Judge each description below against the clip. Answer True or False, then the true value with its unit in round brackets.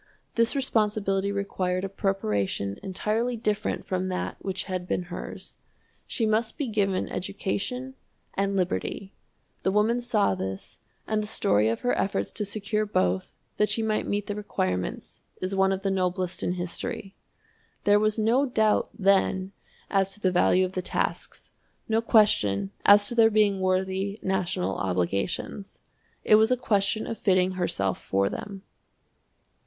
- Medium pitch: False (195 Hz)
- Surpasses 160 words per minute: False (155 wpm)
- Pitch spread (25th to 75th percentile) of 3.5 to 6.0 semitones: False (2.6 semitones)